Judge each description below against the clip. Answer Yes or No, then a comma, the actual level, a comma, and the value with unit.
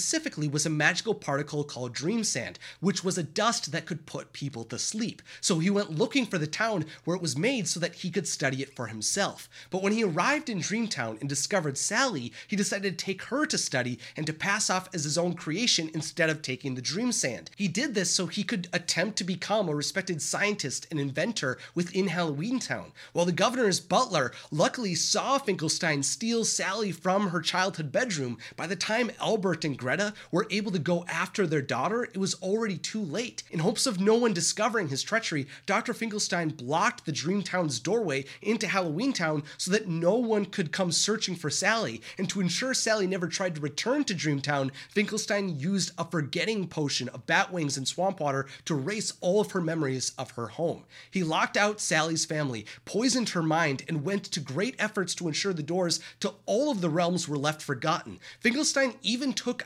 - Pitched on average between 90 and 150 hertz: No, medium, 180 Hz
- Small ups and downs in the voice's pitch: No, average, 5.2 semitones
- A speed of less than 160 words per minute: No, average, 200 wpm